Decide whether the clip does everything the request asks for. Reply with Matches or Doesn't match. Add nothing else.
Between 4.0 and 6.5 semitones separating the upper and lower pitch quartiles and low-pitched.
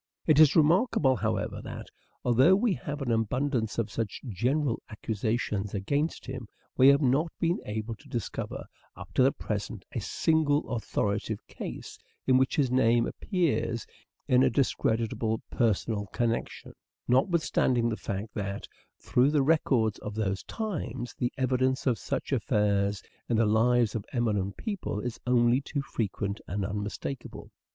Matches